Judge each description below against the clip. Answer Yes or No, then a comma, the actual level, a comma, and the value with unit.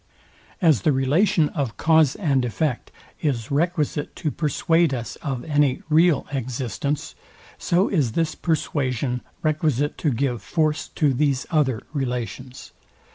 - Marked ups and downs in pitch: No, average, 3.6 semitones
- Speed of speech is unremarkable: No, slow, 130 wpm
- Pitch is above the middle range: No, medium, 145 Hz